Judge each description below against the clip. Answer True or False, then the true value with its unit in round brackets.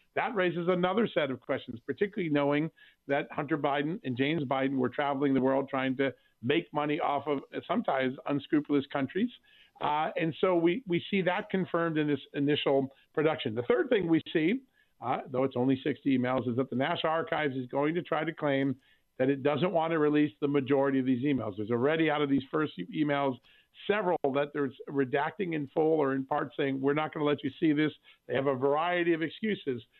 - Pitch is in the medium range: True (145 Hz)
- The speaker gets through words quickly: True (210 wpm)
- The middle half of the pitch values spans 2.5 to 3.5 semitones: True (3.0 semitones)